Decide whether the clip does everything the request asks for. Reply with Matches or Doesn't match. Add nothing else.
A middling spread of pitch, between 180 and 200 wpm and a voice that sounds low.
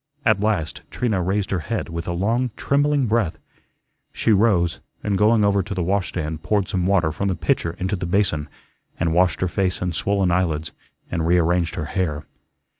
Matches